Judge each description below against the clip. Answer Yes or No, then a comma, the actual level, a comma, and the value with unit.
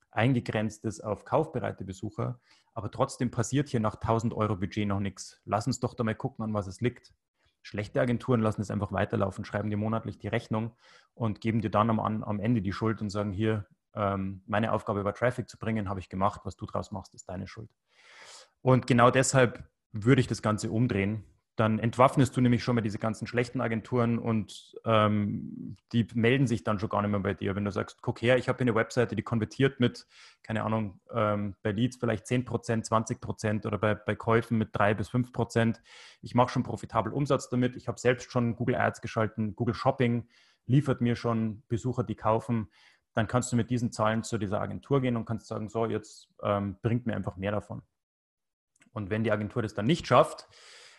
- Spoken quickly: Yes, fast, 200 wpm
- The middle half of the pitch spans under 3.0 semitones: Yes, narrow, 2.4 semitones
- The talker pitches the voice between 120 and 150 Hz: No, low, 110 Hz